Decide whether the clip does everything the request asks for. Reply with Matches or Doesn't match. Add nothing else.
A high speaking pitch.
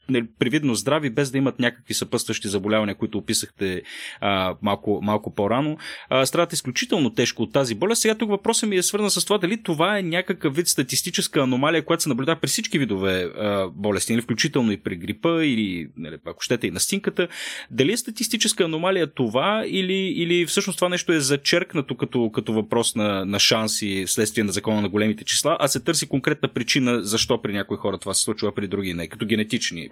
Doesn't match